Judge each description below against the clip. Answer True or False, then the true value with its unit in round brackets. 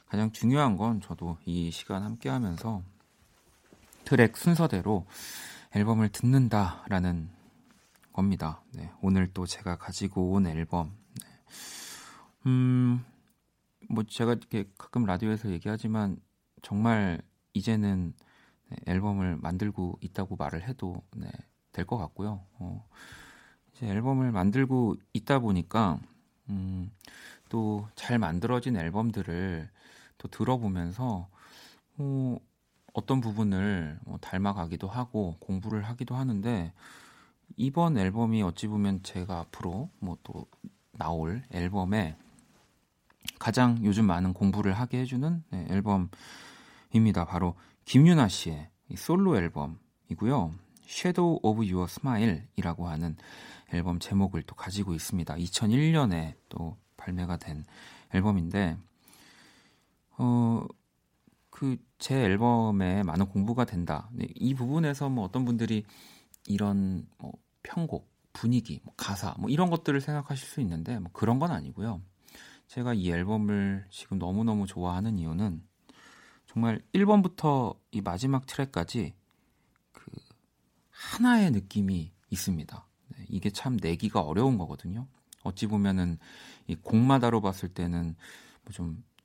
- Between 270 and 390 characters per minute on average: False (250 characters per minute)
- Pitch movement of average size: True (4.8 semitones)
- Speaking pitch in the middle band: False (100 Hz)